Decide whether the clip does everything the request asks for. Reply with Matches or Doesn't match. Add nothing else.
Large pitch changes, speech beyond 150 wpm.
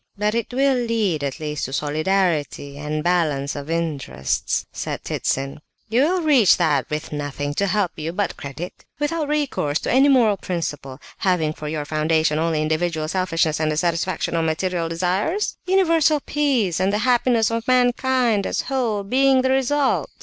Matches